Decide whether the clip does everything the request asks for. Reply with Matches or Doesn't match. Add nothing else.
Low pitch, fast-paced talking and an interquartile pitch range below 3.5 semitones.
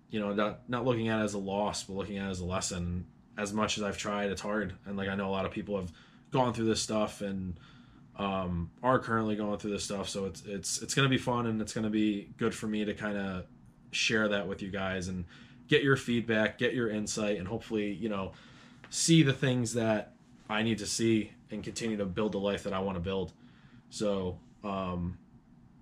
Matches